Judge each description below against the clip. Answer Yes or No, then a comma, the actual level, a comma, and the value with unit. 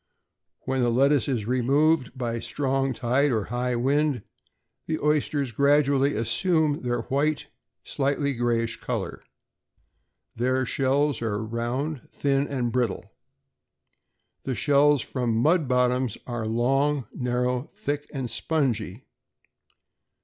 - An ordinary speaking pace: No, slow, 115 wpm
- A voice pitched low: Yes, low, 130 Hz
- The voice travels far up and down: No, average, 3.1 semitones